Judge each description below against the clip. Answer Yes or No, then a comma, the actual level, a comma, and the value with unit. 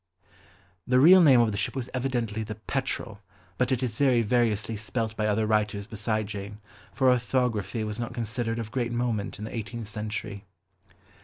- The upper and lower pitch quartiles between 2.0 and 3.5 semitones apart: Yes, narrow, 2.5 semitones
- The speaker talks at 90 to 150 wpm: No, average, 175 wpm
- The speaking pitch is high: No, low, 115 Hz